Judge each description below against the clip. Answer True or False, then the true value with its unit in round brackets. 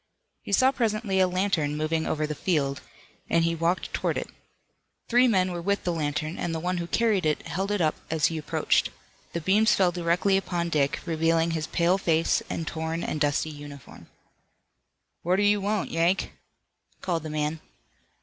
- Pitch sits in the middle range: True (170 Hz)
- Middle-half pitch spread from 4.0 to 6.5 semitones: False (3.3 semitones)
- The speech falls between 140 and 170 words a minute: False (180 wpm)